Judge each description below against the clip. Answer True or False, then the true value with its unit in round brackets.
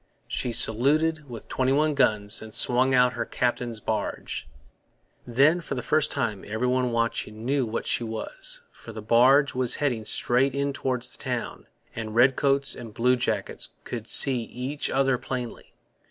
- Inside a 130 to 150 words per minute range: False (160 wpm)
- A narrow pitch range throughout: False (3.0 semitones)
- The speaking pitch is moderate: False (125 Hz)